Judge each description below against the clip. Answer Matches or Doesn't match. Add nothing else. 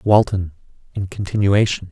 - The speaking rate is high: Doesn't match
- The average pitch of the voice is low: Matches